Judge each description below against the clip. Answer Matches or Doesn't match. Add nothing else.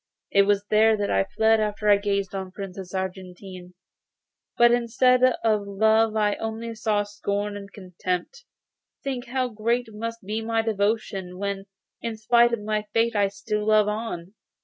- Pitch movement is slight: Matches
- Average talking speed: Matches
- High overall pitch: Matches